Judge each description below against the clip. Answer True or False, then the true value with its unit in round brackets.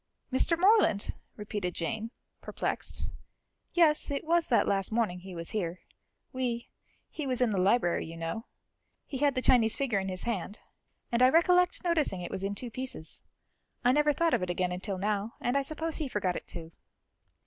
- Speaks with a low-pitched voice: False (230 Hz)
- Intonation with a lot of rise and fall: True (6.9 semitones)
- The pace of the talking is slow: False (185 wpm)